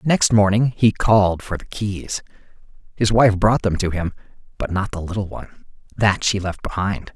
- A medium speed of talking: Yes, average, 185 wpm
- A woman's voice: No, male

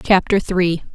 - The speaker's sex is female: Yes, female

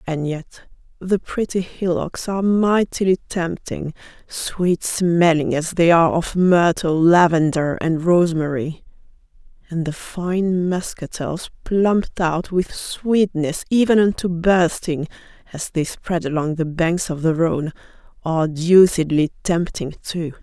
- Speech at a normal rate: No, slow, 125 wpm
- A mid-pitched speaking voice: Yes, medium, 170 Hz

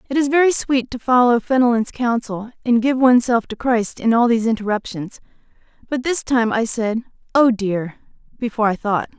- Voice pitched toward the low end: No, high, 235 Hz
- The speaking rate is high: No, average, 175 wpm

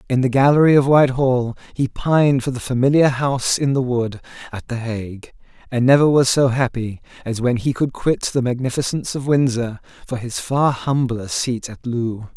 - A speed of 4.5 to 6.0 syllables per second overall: Yes, 5.1 syllables/s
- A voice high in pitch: No, low, 125 Hz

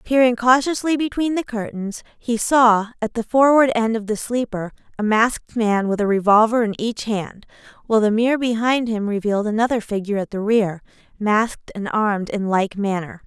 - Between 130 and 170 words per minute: No, average, 180 wpm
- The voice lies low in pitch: No, high, 220 Hz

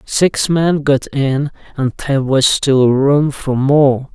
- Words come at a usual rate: Yes, average, 160 wpm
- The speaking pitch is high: No, medium, 140 Hz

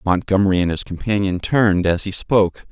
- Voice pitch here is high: No, very low, 95 Hz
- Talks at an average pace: Yes, average, 175 wpm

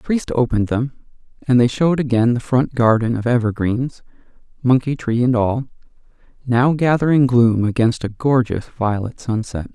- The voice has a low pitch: Yes, low, 125 Hz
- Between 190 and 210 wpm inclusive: No, average, 155 wpm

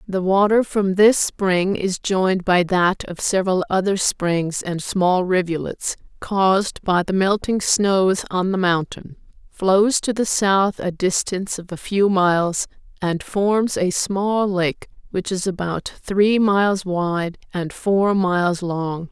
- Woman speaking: Yes, female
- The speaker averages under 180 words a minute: Yes, average, 155 wpm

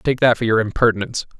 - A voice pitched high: No, low, 115 Hz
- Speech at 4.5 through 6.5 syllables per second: No, 7.1 syllables/s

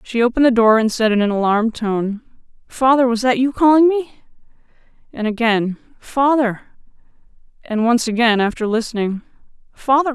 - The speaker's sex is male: No, female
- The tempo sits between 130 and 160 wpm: Yes, average, 150 wpm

